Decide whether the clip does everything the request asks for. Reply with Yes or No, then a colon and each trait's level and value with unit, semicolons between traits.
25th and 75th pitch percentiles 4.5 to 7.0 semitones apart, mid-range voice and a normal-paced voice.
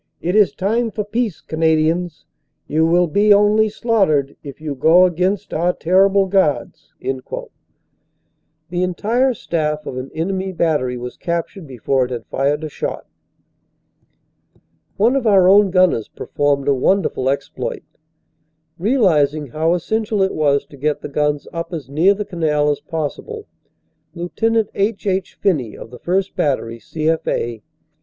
Yes: average, 5.1 semitones; medium, 170 Hz; average, 145 wpm